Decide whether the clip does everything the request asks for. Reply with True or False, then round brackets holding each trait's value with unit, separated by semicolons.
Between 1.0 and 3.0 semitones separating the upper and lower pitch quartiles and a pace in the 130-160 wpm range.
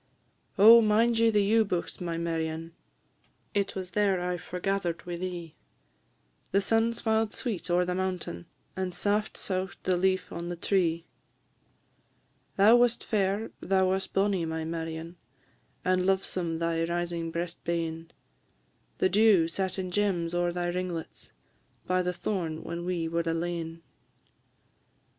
True (2.7 semitones; 140 wpm)